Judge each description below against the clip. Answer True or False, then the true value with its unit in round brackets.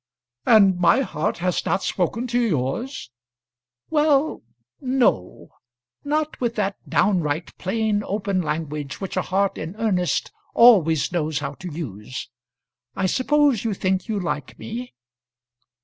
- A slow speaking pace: True (130 wpm)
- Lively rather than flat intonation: True (6.3 semitones)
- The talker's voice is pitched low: False (195 Hz)